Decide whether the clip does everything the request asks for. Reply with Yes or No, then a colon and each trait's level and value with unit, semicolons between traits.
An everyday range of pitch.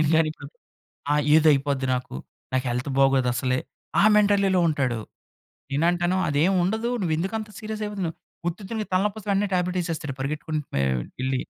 No: wide, 6.1 semitones